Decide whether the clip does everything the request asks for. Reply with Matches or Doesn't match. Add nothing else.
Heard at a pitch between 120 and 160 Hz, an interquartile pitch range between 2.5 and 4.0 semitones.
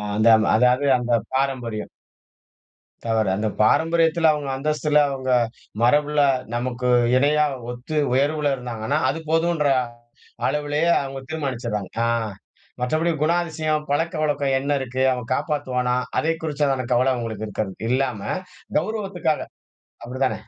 Matches